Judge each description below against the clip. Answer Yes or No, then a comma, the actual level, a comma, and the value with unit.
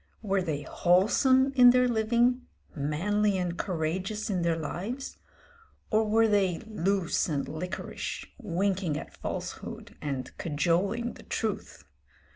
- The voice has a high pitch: Yes, high, 195 Hz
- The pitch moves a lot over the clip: No, average, 4.7 semitones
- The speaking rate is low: Yes, slow, 120 wpm